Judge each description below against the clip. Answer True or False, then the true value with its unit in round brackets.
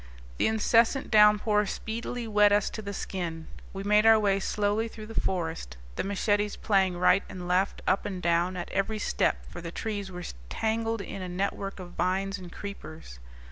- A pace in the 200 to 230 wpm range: False (180 wpm)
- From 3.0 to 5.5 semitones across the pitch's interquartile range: False (2.6 semitones)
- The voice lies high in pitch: True (200 Hz)